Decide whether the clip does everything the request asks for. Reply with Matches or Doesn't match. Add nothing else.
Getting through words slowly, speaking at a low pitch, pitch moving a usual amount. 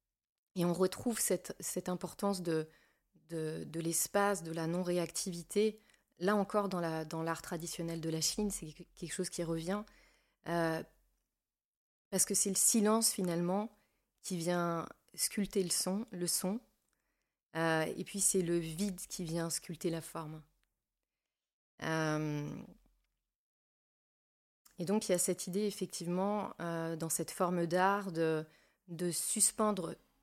Doesn't match